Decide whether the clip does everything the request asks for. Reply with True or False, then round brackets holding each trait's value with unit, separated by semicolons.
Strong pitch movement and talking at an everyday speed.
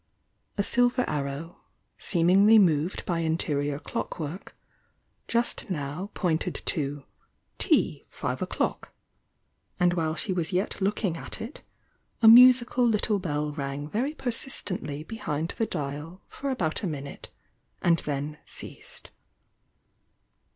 False (6.1 semitones; 120 wpm)